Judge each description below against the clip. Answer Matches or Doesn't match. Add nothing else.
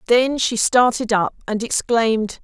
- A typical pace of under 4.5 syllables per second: Matches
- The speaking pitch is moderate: Doesn't match